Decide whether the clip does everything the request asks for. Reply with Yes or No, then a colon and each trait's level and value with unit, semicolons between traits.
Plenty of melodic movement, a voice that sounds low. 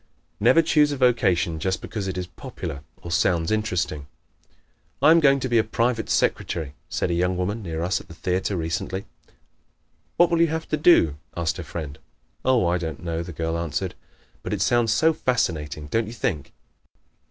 Yes: wide, 6.3 semitones; very low, 95 Hz